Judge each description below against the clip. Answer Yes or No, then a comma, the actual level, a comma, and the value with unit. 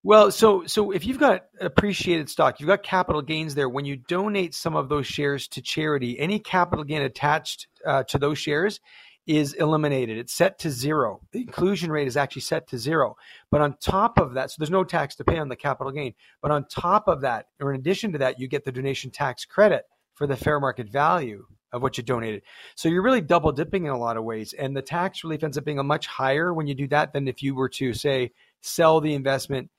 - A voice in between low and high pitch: Yes, medium, 150 Hz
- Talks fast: Yes, fast, 235 wpm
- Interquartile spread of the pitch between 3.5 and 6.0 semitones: Yes, average, 4.3 semitones